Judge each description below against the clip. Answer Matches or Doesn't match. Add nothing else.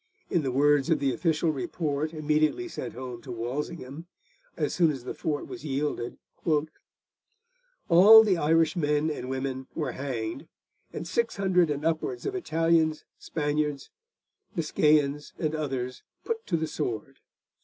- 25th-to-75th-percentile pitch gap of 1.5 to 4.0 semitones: Matches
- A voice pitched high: Doesn't match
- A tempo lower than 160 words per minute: Matches